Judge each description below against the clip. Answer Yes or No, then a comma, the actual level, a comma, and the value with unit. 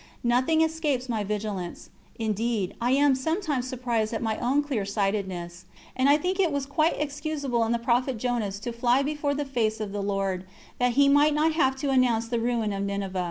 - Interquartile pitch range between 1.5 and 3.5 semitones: No, average, 4.9 semitones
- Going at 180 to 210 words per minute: Yes, average, 200 wpm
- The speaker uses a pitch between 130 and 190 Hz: No, high, 245 Hz